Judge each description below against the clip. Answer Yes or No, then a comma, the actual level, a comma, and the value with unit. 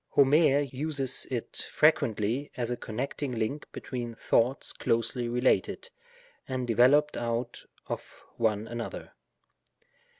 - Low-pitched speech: Yes, low, 125 Hz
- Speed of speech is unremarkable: No, slow, 105 wpm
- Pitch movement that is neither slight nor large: Yes, average, 3.1 semitones